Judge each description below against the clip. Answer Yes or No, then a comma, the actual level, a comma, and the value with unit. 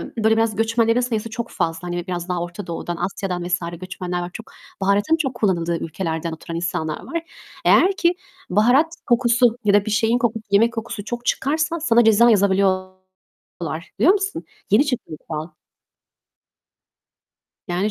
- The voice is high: Yes, high, 205 Hz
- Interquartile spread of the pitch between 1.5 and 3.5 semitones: No, average, 5.0 semitones